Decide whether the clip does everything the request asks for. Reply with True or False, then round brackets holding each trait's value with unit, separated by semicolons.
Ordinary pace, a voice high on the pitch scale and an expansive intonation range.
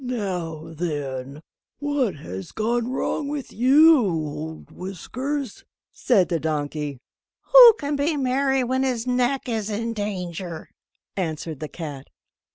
False (125 wpm; 205 Hz; 8.6 semitones)